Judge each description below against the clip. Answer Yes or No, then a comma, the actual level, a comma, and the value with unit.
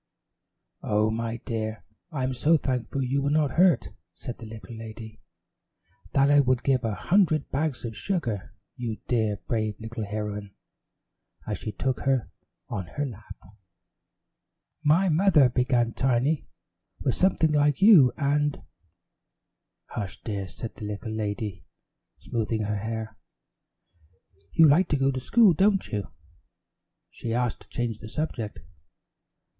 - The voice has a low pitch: Yes, low, 125 Hz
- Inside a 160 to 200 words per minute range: No, average, 140 wpm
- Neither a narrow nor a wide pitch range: Yes, average, 4.9 semitones